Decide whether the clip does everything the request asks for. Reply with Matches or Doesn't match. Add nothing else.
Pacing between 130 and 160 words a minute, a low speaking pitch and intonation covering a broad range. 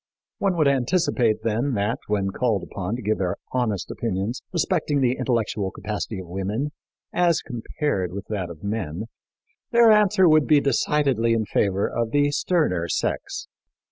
Matches